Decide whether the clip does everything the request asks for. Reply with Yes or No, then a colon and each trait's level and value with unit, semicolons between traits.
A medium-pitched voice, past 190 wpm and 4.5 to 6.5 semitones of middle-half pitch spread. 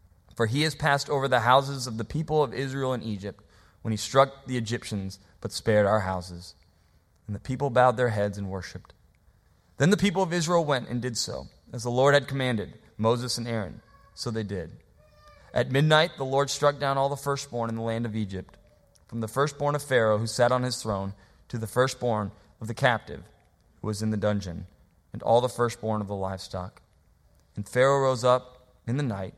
No: low, 115 Hz; fast, 205 wpm; average, 5.1 semitones